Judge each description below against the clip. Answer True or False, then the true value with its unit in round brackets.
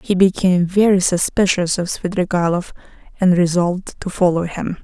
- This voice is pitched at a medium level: True (180 Hz)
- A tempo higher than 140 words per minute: False (135 wpm)